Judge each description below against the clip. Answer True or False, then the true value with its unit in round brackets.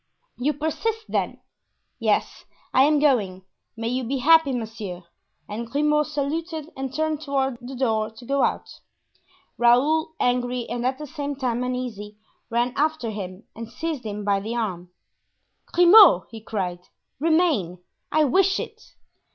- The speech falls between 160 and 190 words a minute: False (145 wpm)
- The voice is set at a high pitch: True (255 Hz)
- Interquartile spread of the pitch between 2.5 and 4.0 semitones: False (5.1 semitones)